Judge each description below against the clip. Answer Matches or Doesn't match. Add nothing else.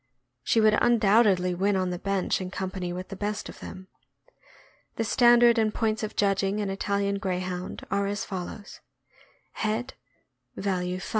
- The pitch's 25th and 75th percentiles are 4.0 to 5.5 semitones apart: Doesn't match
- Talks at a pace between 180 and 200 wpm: Doesn't match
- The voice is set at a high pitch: Matches